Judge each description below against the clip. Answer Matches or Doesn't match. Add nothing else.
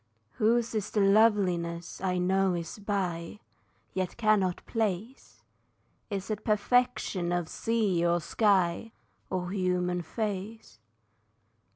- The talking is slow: Matches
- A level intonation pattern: Doesn't match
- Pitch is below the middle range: Doesn't match